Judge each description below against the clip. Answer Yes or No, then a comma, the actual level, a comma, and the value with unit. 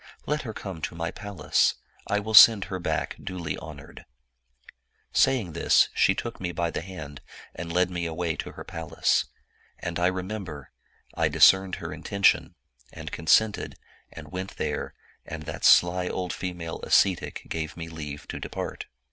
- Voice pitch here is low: Yes, very low, 90 Hz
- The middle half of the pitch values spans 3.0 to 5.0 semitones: No, narrow, 2.6 semitones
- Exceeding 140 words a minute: Yes, average, 165 wpm